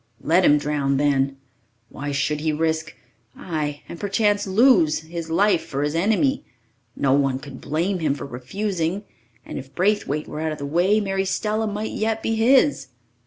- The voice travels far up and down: Yes, wide, 5.9 semitones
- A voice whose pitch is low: No, medium, 160 Hz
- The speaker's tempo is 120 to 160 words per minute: No, average, 170 wpm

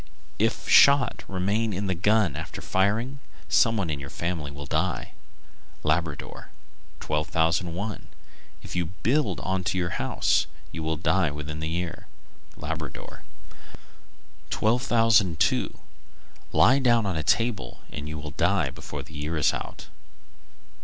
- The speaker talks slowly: Yes, slow, 130 wpm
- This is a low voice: Yes, very low, 85 Hz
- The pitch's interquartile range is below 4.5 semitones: No, wide, 5.6 semitones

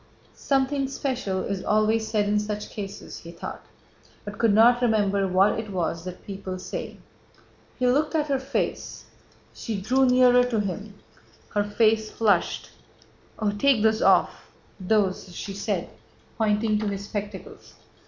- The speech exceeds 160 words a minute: No, average, 145 wpm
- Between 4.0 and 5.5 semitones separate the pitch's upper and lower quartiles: No, average, 3.4 semitones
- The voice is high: Yes, high, 210 Hz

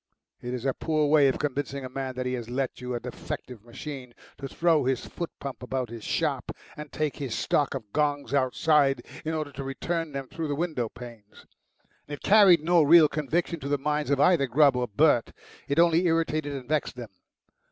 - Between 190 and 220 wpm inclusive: Yes, fast, 205 wpm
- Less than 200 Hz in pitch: Yes, medium, 140 Hz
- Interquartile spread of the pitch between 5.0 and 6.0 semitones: No, average, 3.4 semitones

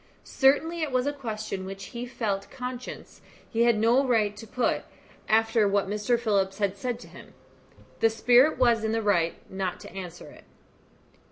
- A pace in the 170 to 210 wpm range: Yes, average, 175 wpm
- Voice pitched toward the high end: Yes, high, 225 Hz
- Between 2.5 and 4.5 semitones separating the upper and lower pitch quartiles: Yes, average, 3.6 semitones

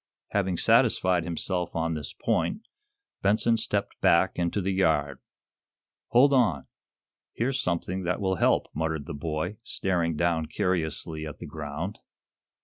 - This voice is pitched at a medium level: No, very low, 85 Hz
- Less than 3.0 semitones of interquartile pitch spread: No, average, 3.4 semitones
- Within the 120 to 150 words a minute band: Yes, slow, 135 wpm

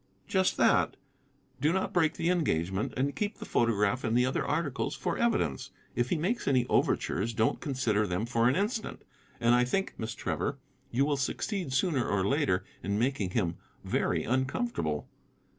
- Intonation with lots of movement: Yes, wide, 6.5 semitones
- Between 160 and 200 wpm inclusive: Yes, average, 165 wpm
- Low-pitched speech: Yes, low, 130 Hz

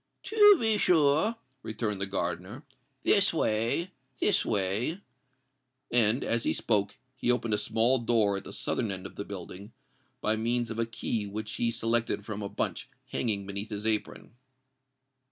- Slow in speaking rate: No, average, 155 wpm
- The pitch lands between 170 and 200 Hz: No, low, 110 Hz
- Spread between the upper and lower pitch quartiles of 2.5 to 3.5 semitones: Yes, average, 3.2 semitones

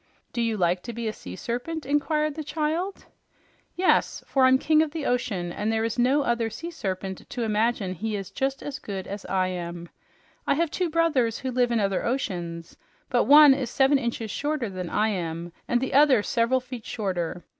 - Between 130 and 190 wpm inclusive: No, average, 200 wpm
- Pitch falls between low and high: No, high, 235 Hz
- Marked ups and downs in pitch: Yes, wide, 6.4 semitones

